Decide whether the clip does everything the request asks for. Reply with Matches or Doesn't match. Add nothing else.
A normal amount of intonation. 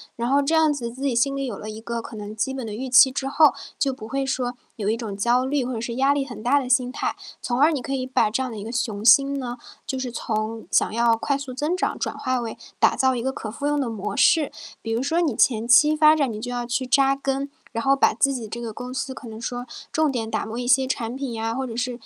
Matches